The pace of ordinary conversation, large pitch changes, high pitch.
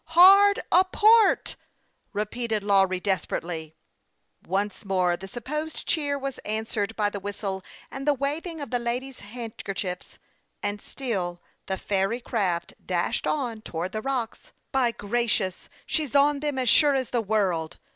Yes: average, 155 wpm; wide, 6.1 semitones; high, 225 Hz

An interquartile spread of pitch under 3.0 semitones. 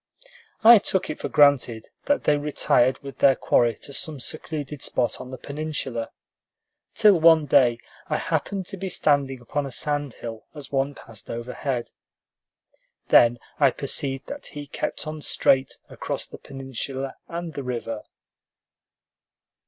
No: average, 3.3 semitones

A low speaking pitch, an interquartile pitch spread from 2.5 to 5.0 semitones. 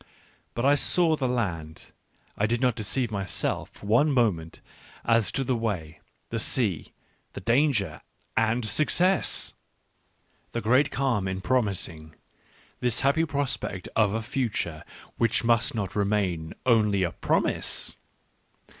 Yes: low, 115 Hz; average, 4.7 semitones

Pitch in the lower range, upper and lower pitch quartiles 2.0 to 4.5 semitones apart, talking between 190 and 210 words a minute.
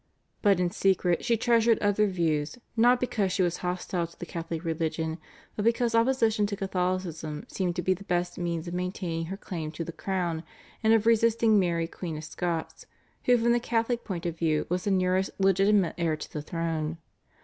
No: medium, 180 Hz; average, 4.1 semitones; average, 195 wpm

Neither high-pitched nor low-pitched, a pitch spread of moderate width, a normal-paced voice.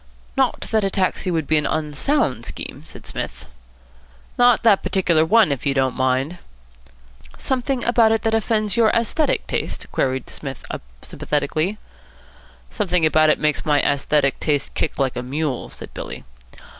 No: medium, 160 Hz; wide, 7.6 semitones; average, 155 wpm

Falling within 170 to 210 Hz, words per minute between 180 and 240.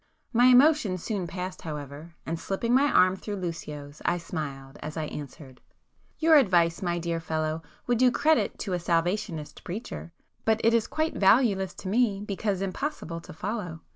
No: medium, 185 Hz; average, 165 wpm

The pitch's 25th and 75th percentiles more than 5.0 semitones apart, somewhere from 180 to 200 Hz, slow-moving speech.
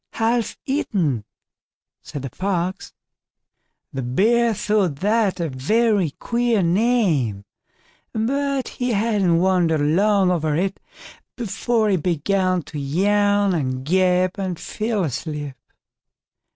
Yes: wide, 5.4 semitones; high, 190 Hz; slow, 110 wpm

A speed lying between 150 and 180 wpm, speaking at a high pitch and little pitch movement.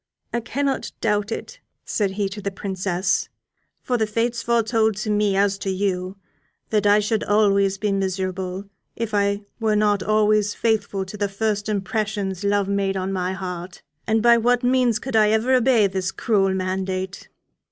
Yes: average, 170 wpm; high, 205 Hz; narrow, 2.3 semitones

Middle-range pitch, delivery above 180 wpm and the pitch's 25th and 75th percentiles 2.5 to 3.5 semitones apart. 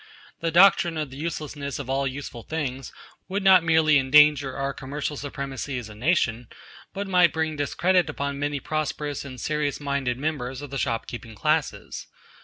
No: medium, 145 Hz; average, 170 wpm; average, 2.8 semitones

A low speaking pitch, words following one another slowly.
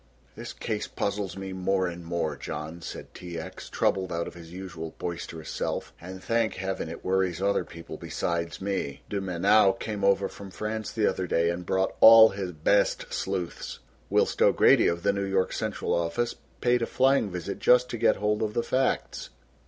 No: very low, 95 Hz; average, 185 wpm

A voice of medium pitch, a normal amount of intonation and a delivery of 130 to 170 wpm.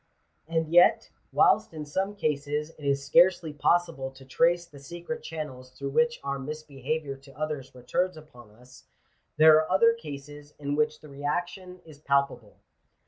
Yes: medium, 150 Hz; average, 3.3 semitones; average, 160 wpm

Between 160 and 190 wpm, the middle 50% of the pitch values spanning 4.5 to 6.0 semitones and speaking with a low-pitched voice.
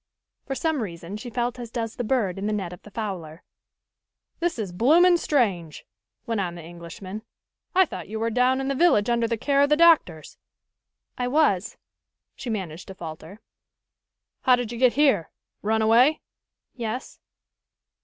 No: average, 170 wpm; wide, 5.6 semitones; high, 225 Hz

